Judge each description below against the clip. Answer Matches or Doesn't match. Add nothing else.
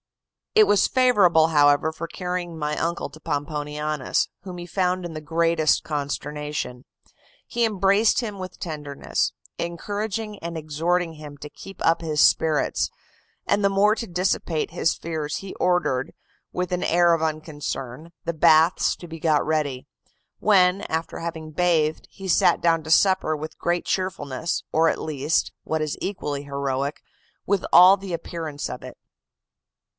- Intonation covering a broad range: Doesn't match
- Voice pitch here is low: Doesn't match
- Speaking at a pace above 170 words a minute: Doesn't match